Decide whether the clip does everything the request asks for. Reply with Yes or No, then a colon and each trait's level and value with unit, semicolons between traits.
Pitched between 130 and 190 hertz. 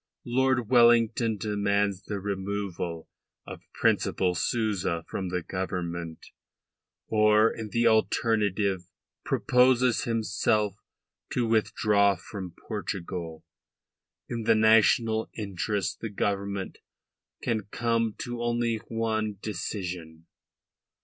No: low, 105 Hz